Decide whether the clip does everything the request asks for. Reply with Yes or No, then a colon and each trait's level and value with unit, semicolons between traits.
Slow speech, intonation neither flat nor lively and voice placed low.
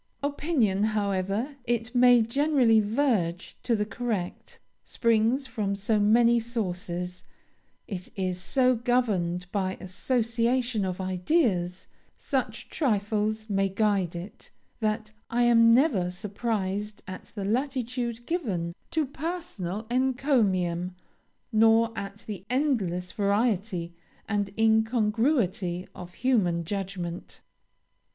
No: slow, 105 wpm; average, 4.3 semitones; high, 215 Hz